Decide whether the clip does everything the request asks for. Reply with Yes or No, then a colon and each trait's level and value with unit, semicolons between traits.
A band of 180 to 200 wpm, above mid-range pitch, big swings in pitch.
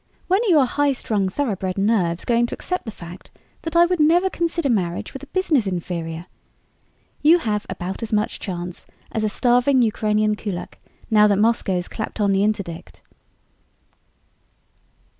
No: average, 160 wpm; high, 215 Hz; wide, 6.7 semitones